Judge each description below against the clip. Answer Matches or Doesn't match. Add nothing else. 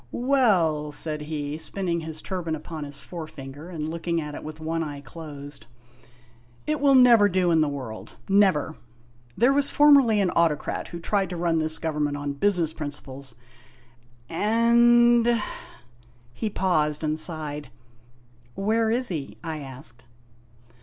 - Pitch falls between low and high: Matches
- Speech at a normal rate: Matches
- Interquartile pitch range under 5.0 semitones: Doesn't match